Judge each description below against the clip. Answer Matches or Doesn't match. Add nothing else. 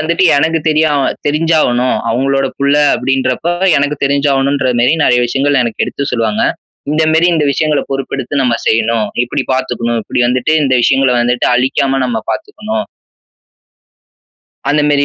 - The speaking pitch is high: Doesn't match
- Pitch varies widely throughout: Doesn't match